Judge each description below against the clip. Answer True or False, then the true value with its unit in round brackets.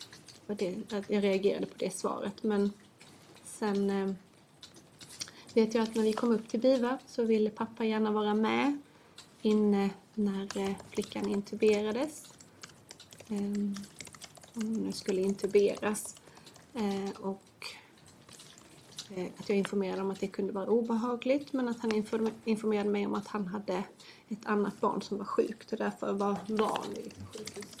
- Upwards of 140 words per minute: False (135 wpm)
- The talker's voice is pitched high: True (210 Hz)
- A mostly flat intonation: True (1.8 semitones)